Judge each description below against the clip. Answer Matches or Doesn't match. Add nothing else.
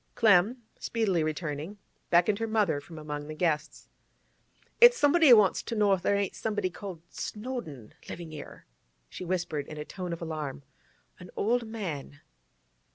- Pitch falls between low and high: Matches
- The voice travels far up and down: Matches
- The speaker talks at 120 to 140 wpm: Doesn't match